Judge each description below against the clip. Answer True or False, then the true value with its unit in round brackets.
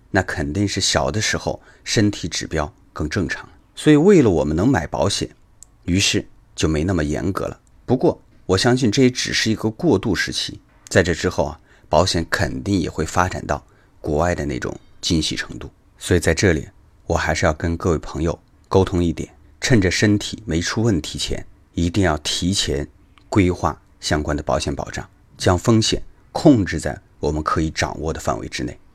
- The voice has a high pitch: False (90 Hz)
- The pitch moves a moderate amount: True (4.3 semitones)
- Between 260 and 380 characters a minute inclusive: True (270 characters per minute)